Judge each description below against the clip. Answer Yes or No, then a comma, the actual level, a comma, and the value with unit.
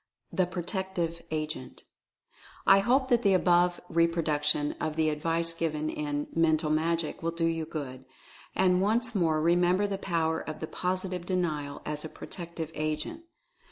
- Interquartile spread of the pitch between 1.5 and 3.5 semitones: Yes, average, 2.8 semitones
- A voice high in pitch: No, medium, 165 Hz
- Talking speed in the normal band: Yes, average, 150 wpm